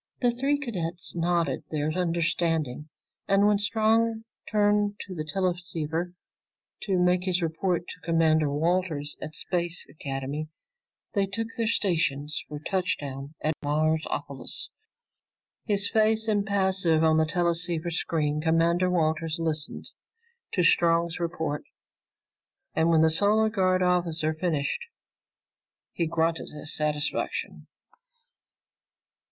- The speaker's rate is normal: No, slow, 115 wpm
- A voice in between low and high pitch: Yes, medium, 170 Hz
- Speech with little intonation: No, average, 3.2 semitones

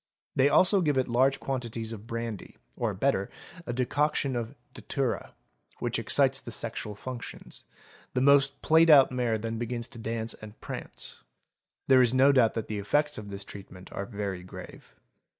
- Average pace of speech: Yes, average, 170 wpm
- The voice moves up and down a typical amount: Yes, average, 3.7 semitones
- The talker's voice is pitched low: Yes, low, 120 Hz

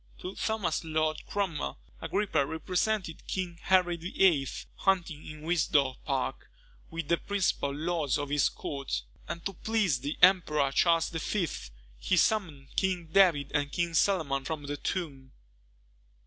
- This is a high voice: No, medium, 165 Hz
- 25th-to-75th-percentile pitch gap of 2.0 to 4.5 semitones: Yes, average, 4.2 semitones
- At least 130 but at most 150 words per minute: Yes, slow, 135 wpm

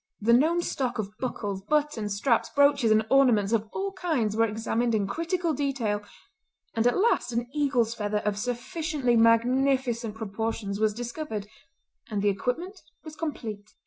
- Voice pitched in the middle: No, high, 235 Hz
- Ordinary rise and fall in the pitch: Yes, average, 4.8 semitones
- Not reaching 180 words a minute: Yes, average, 150 wpm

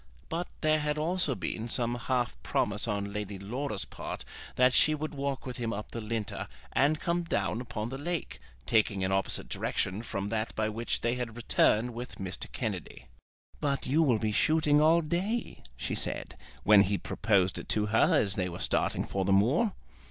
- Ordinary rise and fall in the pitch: No, wide, 6.1 semitones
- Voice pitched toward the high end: No, low, 115 Hz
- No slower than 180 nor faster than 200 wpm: Yes, average, 190 wpm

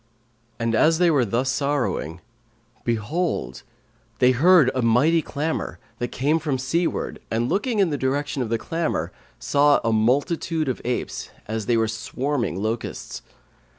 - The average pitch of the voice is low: Yes, low, 130 Hz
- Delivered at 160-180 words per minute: No, average, 150 wpm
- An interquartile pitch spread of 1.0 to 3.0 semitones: No, average, 5.3 semitones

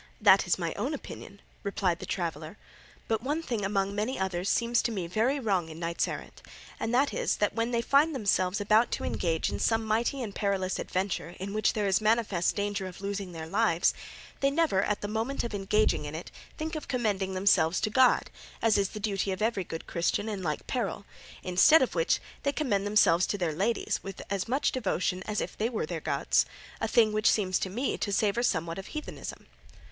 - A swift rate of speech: Yes, fast, 210 wpm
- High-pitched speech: Yes, high, 205 Hz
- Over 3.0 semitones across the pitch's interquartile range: Yes, average, 3.6 semitones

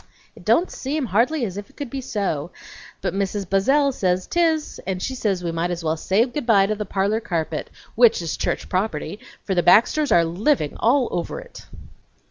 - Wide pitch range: Yes, wide, 6.7 semitones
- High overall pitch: Yes, high, 205 Hz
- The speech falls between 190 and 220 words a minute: Yes, average, 200 wpm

